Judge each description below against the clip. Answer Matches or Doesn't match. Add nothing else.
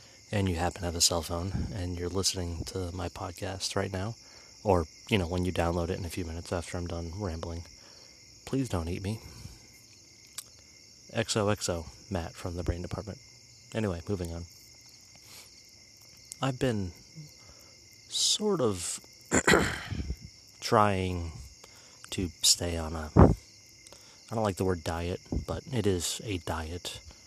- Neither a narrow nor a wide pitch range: Matches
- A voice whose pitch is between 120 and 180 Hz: Doesn't match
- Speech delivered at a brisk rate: Doesn't match